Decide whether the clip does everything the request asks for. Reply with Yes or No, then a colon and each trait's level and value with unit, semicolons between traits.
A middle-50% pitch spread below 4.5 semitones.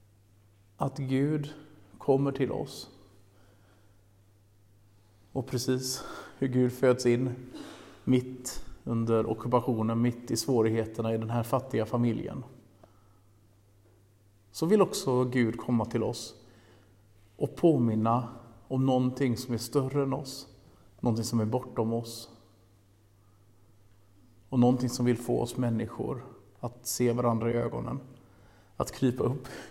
Yes: average, 3.8 semitones